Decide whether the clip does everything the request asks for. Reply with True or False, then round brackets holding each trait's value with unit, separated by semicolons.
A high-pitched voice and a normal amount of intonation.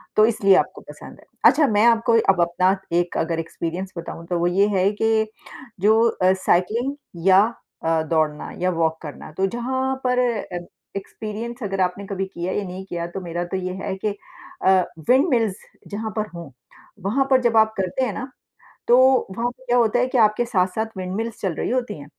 True (195 Hz; 4.2 semitones)